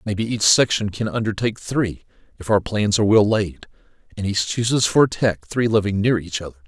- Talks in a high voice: No, low, 105 Hz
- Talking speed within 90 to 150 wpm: No, average, 200 wpm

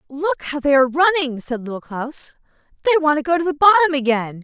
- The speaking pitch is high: Yes, very high, 295 Hz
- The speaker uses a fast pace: Yes, fast, 215 wpm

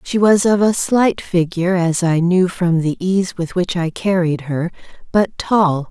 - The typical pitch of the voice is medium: Yes, medium, 180 Hz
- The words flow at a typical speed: Yes, average, 195 wpm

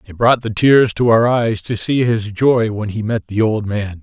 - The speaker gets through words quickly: Yes, fast, 255 wpm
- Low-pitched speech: Yes, low, 110 Hz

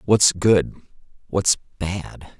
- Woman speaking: No, male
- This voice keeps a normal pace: No, slow, 100 wpm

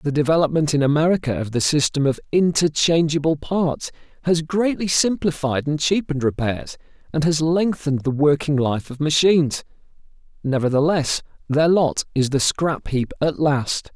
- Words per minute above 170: No, average, 140 wpm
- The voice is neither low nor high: Yes, medium, 150 Hz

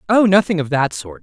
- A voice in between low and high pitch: Yes, medium, 160 Hz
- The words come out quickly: Yes, fast, 245 wpm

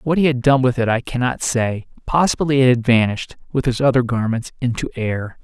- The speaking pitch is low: Yes, low, 125 Hz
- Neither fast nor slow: No, fast, 210 wpm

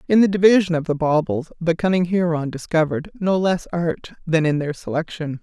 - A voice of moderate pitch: Yes, medium, 170 Hz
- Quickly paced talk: No, average, 190 wpm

